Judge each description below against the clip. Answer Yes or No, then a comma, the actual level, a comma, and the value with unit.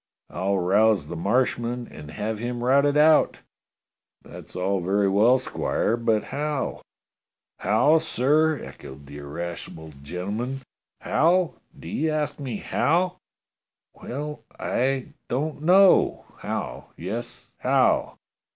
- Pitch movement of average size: No, wide, 7.2 semitones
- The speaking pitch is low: Yes, low, 120 Hz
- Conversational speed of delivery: No, slow, 120 wpm